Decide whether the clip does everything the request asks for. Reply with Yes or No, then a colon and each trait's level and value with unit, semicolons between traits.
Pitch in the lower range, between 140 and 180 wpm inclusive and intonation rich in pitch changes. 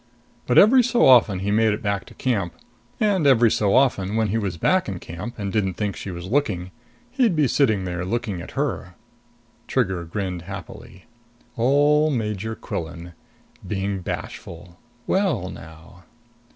Yes: low, 105 Hz; average, 155 wpm; wide, 5.9 semitones